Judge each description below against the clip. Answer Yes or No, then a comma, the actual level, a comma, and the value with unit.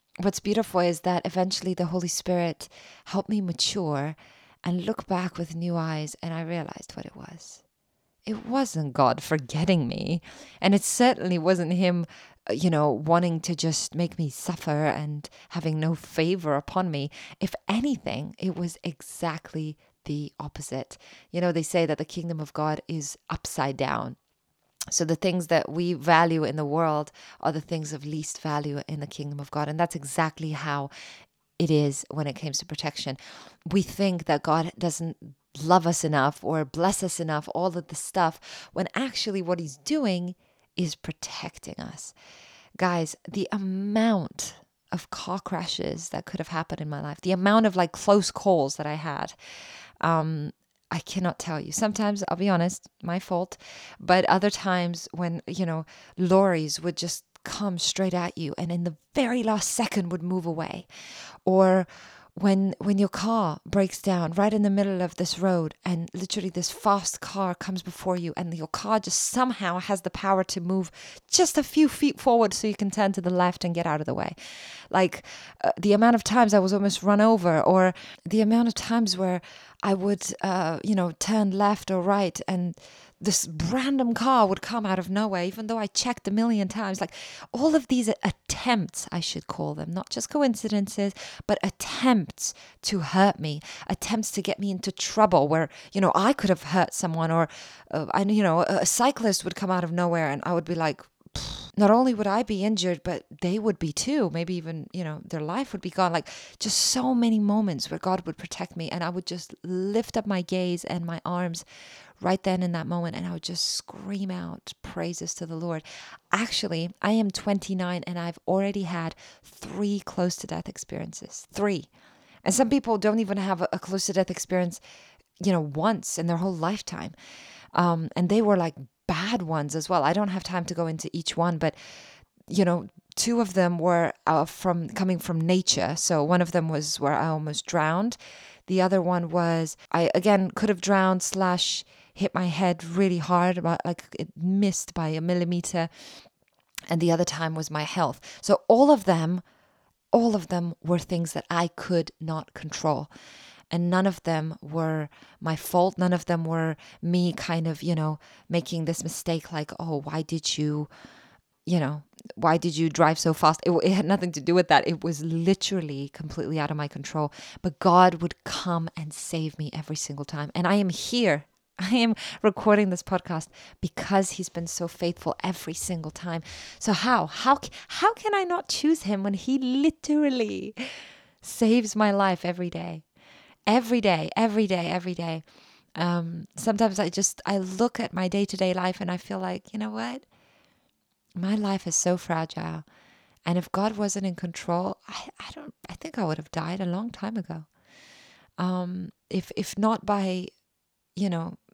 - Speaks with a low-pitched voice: No, medium, 180 Hz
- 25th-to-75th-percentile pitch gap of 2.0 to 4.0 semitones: Yes, average, 3.5 semitones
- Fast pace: No, average, 185 wpm